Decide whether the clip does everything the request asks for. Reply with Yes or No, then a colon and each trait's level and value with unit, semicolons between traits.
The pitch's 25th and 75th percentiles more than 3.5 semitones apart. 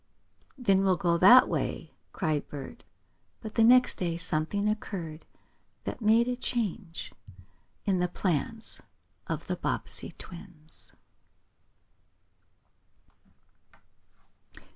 Yes: average, 5.1 semitones